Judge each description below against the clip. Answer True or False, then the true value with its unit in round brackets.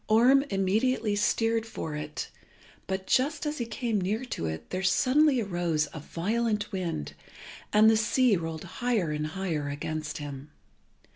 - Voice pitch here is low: False (195 Hz)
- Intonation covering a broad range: True (6.5 semitones)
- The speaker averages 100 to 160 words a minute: True (150 wpm)